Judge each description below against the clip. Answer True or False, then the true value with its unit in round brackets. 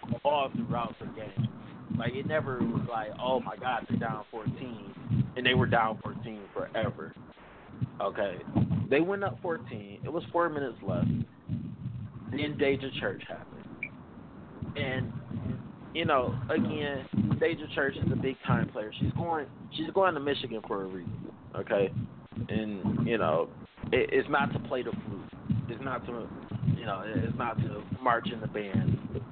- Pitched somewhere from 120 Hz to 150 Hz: True (135 Hz)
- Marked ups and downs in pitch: True (6.8 semitones)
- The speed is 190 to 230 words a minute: False (160 wpm)